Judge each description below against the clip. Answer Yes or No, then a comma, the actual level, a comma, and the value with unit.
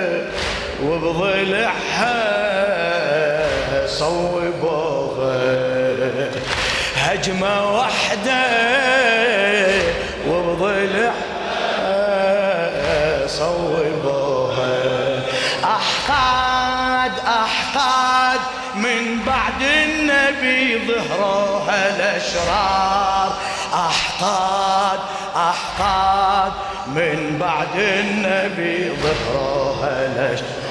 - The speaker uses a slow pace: Yes, slow, 40 wpm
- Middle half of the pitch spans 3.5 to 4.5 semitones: Yes, average, 4.1 semitones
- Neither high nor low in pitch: No, high, 195 Hz